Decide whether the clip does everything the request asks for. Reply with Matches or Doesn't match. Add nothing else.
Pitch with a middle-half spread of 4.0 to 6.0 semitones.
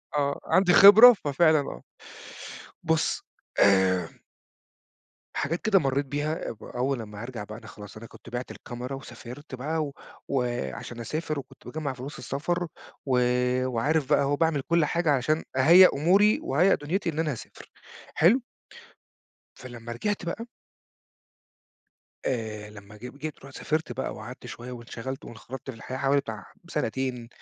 Matches